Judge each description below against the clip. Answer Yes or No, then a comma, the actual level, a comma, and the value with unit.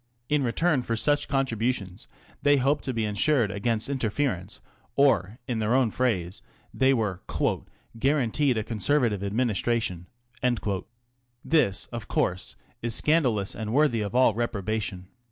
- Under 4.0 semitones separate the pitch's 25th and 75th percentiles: No, average, 4.6 semitones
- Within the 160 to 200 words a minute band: No, slow, 135 wpm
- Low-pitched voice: Yes, low, 115 Hz